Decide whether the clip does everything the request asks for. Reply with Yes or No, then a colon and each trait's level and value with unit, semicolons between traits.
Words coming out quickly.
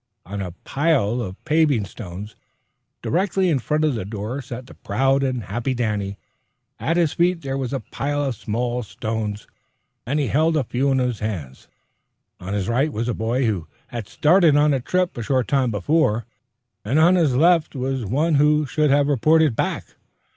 No: average, 185 wpm